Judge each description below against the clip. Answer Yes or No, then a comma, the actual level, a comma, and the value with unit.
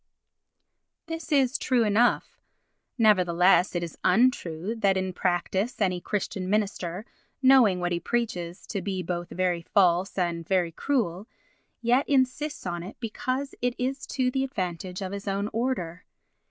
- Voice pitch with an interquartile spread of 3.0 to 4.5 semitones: No, wide, 5.6 semitones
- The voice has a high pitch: Yes, high, 195 Hz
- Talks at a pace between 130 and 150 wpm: Yes, average, 145 wpm